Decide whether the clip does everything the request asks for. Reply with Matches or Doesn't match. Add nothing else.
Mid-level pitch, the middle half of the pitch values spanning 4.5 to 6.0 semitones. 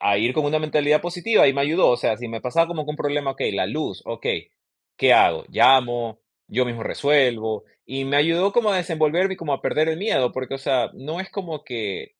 Matches